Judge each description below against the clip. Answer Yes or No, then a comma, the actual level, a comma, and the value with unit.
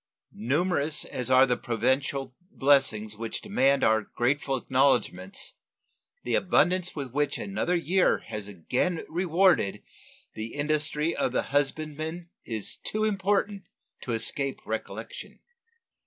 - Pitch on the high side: No, medium, 145 Hz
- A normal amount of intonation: No, wide, 6.0 semitones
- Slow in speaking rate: Yes, slow, 115 wpm